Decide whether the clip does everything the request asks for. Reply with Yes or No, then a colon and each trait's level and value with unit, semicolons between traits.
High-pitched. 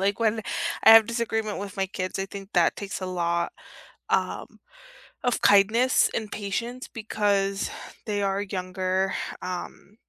Yes: high, 200 Hz